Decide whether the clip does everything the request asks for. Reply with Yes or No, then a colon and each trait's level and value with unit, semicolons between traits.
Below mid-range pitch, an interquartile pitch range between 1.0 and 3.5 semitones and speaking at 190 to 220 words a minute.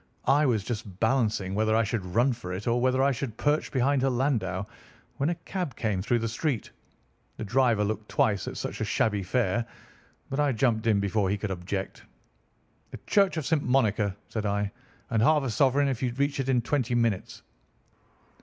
No: low, 115 Hz; average, 4.5 semitones; average, 195 wpm